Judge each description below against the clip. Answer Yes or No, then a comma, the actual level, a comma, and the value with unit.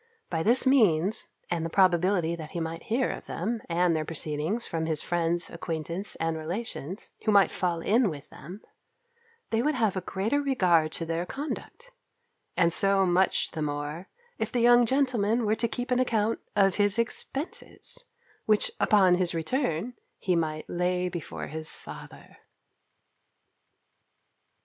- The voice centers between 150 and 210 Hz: Yes, medium, 185 Hz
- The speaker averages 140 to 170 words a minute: Yes, average, 155 wpm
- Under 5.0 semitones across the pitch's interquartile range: No, average, 5.3 semitones